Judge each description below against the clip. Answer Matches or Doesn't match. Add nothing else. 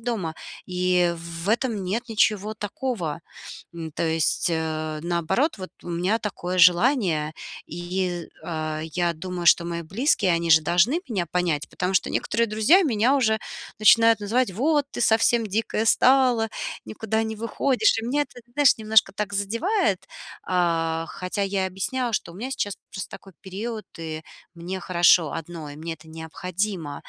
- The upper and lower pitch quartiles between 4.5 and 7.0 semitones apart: Matches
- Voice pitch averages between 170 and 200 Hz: Matches